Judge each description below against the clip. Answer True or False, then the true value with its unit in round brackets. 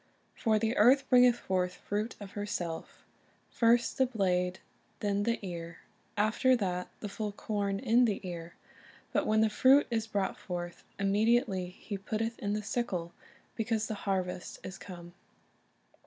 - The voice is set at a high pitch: True (205 Hz)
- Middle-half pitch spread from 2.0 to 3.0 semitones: False (3.6 semitones)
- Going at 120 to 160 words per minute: True (150 wpm)